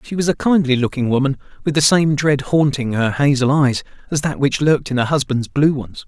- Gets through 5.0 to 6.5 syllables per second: Yes, 5.5 syllables/s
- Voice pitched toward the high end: No, medium, 140 Hz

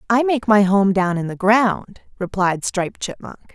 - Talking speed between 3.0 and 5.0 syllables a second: Yes, 4.6 syllables/s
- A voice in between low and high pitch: No, high, 205 Hz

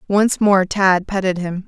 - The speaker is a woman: Yes, female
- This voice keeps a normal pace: Yes, average, 180 wpm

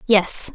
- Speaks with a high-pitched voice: Yes, high, 205 Hz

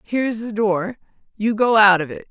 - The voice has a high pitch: Yes, high, 210 Hz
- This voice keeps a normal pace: No, fast, 210 wpm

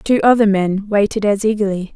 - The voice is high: Yes, high, 205 Hz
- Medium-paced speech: Yes, average, 185 wpm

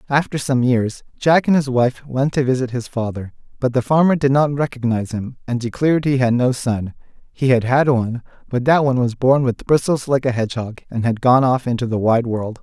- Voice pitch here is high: No, low, 130 Hz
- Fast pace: Yes, fast, 225 wpm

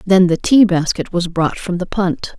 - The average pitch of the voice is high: No, medium, 180 Hz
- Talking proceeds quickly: Yes, fast, 225 wpm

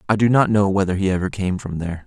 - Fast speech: Yes, fast, 290 wpm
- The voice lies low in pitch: Yes, low, 100 Hz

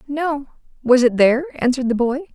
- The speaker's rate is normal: Yes, average, 180 wpm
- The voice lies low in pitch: No, very high, 270 Hz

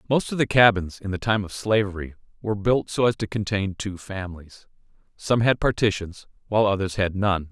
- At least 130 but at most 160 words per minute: No, average, 190 wpm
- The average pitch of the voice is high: No, low, 100 Hz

